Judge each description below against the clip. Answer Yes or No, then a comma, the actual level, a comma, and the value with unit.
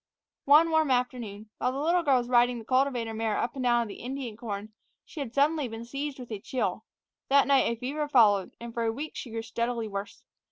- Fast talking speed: Yes, fast, 230 wpm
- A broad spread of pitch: No, average, 3.5 semitones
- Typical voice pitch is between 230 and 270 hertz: Yes, high, 245 Hz